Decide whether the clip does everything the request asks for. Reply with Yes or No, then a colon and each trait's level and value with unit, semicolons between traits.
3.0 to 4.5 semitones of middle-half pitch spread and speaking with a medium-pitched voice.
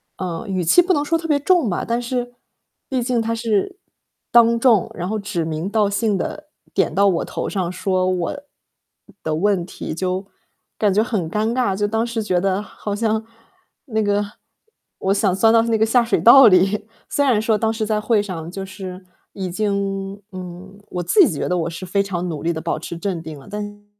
No: average, 3.6 semitones; high, 205 Hz